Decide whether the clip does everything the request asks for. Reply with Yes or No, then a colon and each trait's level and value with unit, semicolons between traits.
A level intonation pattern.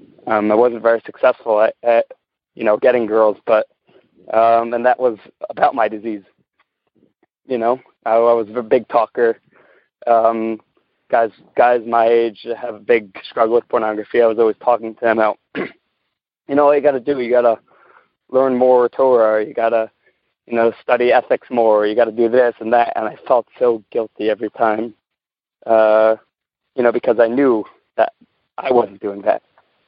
Yes: narrow, 1.8 semitones